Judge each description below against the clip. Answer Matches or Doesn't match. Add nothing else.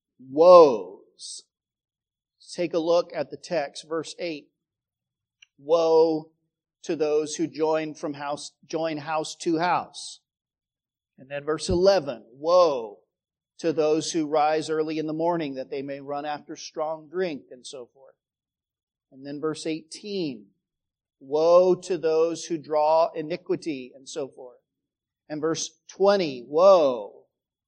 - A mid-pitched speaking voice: Matches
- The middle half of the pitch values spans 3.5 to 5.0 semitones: Doesn't match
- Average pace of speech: Doesn't match